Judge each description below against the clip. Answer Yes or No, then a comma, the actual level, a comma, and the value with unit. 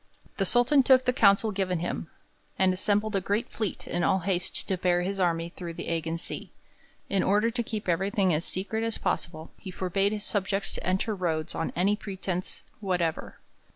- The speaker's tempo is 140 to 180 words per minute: No, average, 190 wpm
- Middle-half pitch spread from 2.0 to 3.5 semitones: Yes, average, 2.9 semitones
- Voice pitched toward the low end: No, high, 190 Hz